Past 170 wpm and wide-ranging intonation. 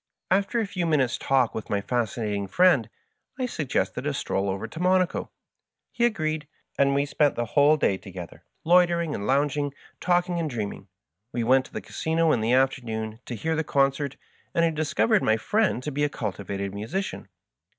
Yes: average, 185 wpm; wide, 6.8 semitones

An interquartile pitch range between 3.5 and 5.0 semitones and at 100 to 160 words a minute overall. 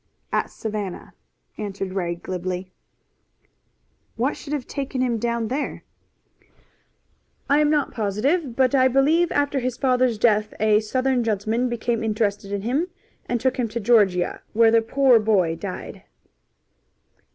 Yes: average, 3.9 semitones; average, 140 wpm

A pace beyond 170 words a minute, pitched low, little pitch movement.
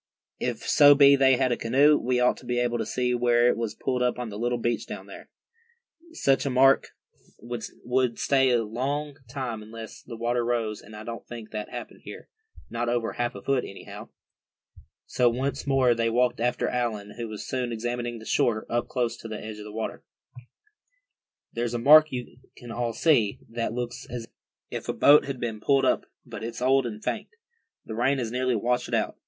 Yes: fast, 205 wpm; low, 120 Hz; narrow, 2.0 semitones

